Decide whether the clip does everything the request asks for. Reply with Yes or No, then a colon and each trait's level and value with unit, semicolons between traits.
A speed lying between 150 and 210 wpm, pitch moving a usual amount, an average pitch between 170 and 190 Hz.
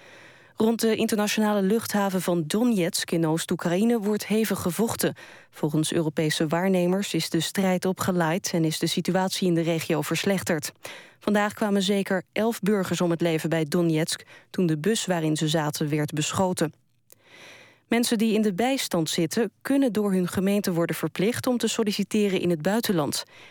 Yes: average, 160 wpm; average, 4.1 semitones; medium, 185 Hz